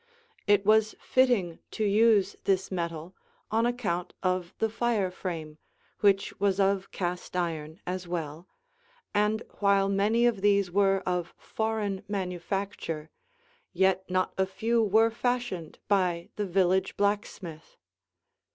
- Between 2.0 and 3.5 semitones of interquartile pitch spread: Yes, average, 2.7 semitones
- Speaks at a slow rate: Yes, slow, 125 wpm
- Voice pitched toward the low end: No, high, 195 Hz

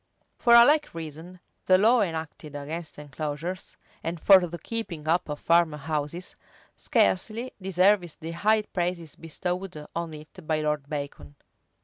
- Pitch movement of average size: Yes, average, 3.5 semitones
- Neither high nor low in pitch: Yes, medium, 165 Hz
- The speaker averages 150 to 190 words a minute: No, average, 140 wpm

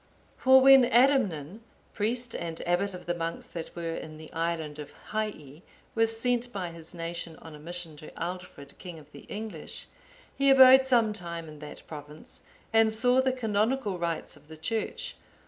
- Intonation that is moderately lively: No, wide, 6.0 semitones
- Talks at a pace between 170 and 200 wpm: Yes, average, 175 wpm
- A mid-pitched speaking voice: Yes, medium, 180 Hz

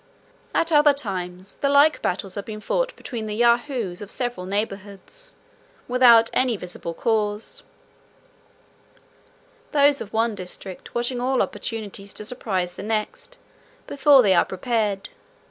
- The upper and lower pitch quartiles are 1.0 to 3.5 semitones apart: No, average, 4.8 semitones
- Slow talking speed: Yes, slow, 130 wpm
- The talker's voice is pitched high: Yes, high, 225 Hz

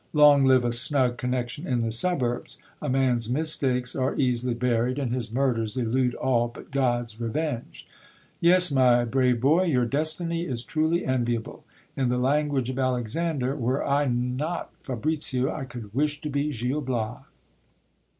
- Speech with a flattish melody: No, average, 3.1 semitones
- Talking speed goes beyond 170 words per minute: No, average, 155 wpm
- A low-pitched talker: Yes, low, 130 Hz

